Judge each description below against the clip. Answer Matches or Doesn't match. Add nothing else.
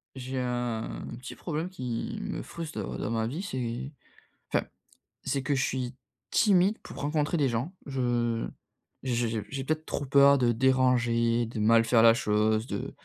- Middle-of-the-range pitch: Doesn't match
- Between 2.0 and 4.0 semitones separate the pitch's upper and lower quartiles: Matches